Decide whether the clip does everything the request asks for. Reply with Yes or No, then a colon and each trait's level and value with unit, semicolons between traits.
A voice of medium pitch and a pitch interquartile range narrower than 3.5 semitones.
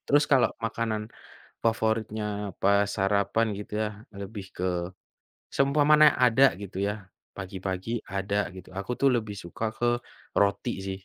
No: low, 105 Hz; average, 2.7 semitones